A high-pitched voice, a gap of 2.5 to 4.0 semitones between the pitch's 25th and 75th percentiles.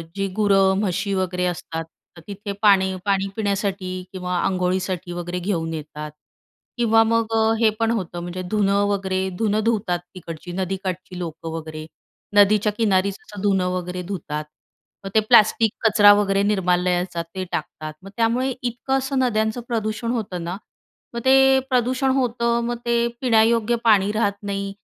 Yes: high, 200 Hz; average, 3.7 semitones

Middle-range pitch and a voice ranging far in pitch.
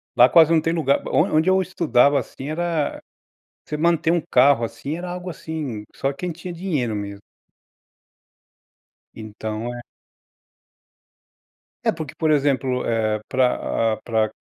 Yes: medium, 145 Hz; wide, 5.8 semitones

